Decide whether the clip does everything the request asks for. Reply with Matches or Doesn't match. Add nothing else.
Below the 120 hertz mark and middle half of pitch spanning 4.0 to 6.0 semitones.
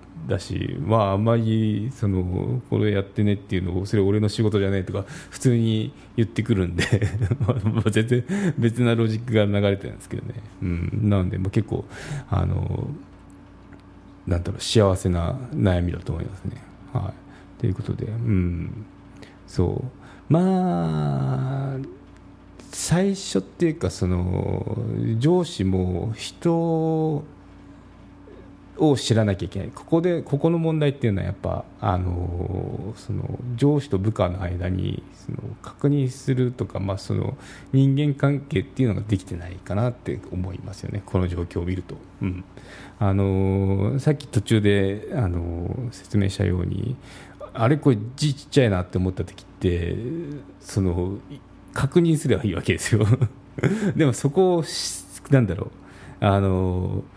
Matches